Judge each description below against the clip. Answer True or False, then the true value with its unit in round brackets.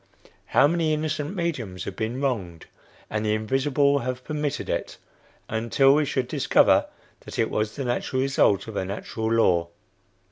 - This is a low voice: True (130 Hz)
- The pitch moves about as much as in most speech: True (5.0 semitones)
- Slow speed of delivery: False (155 wpm)